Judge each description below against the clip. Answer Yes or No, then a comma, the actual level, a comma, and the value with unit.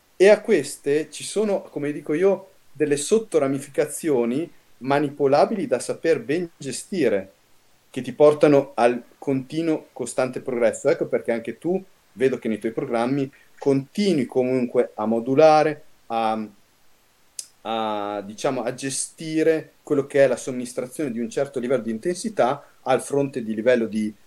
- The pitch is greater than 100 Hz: Yes, medium, 140 Hz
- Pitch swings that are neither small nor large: Yes, average, 4.8 semitones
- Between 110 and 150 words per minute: Yes, average, 140 wpm